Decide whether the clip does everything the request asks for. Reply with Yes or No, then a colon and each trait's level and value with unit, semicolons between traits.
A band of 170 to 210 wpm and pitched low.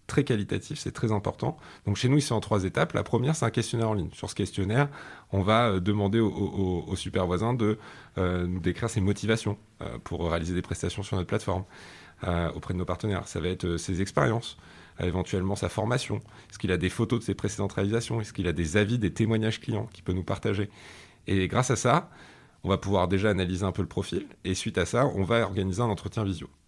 No: fast, 220 wpm; low, 100 Hz